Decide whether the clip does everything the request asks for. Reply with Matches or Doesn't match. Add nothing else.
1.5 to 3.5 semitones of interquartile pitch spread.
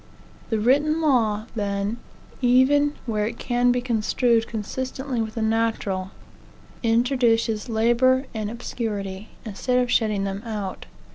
Matches